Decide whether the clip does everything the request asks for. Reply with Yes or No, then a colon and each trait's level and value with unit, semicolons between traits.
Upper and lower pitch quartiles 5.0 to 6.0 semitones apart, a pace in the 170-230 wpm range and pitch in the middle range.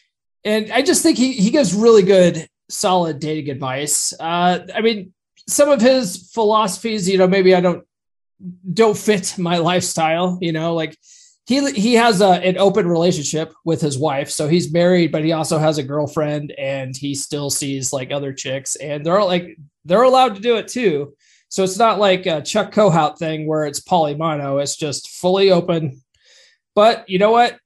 Yes: wide, 5.4 semitones; average, 185 wpm; medium, 180 Hz